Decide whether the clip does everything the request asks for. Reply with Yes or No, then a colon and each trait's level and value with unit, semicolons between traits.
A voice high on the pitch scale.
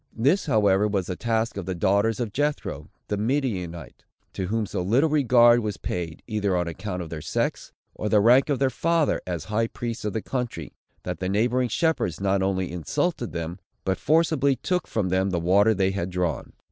No: low, 105 Hz